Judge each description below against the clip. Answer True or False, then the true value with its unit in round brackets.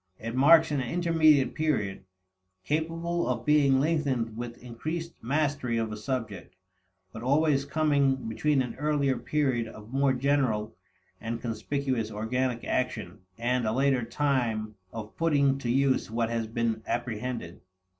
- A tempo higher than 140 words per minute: False (135 wpm)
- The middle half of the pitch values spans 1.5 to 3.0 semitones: False (4.1 semitones)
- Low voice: True (130 Hz)